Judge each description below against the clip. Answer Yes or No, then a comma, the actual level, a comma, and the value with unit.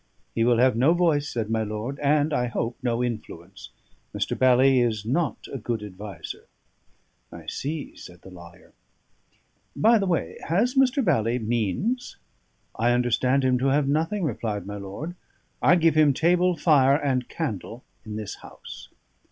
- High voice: No, low, 130 Hz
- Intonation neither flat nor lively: No, wide, 5.9 semitones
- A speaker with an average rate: Yes, average, 160 wpm